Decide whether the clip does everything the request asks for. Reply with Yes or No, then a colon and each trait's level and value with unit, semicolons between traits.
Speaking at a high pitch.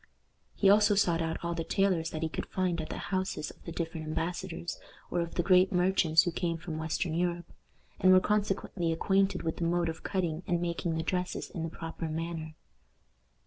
No: medium, 170 Hz